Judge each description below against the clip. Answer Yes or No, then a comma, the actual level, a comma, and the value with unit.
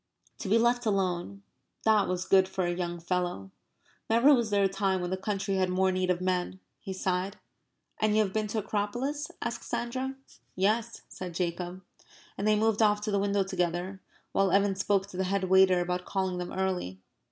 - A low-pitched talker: No, high, 190 Hz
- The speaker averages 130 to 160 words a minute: No, average, 200 wpm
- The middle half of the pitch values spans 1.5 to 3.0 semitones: Yes, narrow, 2.4 semitones